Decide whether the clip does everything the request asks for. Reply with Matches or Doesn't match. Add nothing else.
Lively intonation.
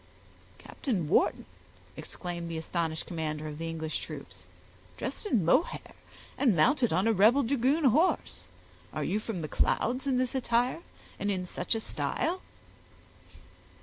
Matches